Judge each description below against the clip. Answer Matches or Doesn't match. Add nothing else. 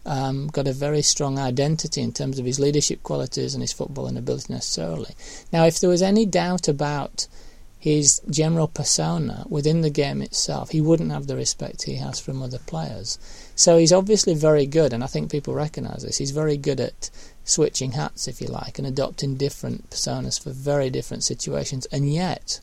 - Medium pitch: Matches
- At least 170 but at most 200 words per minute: Matches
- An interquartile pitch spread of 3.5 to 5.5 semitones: Doesn't match